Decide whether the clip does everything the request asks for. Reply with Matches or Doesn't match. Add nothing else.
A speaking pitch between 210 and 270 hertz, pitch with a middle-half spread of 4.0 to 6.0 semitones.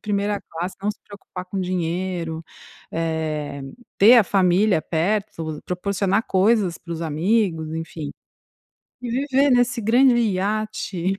Doesn't match